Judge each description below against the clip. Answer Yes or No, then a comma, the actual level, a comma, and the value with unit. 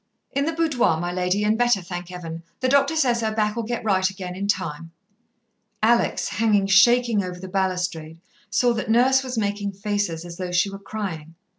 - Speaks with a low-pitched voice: No, high, 200 Hz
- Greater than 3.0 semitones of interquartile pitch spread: Yes, average, 4.6 semitones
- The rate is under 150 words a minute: No, average, 185 wpm